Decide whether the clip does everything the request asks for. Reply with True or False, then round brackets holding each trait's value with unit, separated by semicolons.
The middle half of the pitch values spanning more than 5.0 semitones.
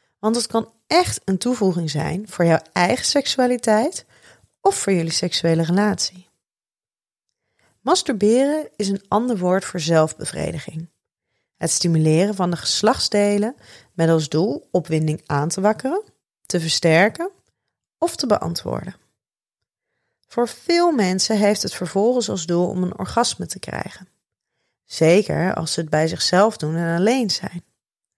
True (5.5 semitones)